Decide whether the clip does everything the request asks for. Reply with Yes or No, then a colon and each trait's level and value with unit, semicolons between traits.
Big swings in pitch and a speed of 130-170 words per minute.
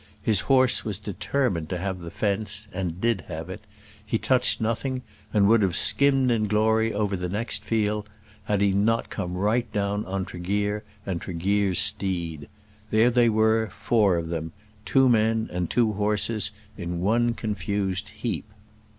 No: average, 3.1 semitones; average, 160 wpm